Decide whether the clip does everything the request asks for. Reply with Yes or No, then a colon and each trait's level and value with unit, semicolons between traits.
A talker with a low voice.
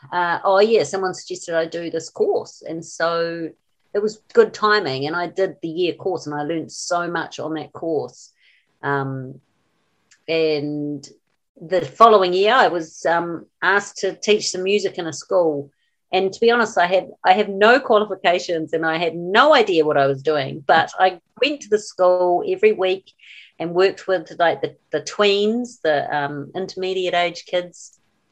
No: medium, 175 Hz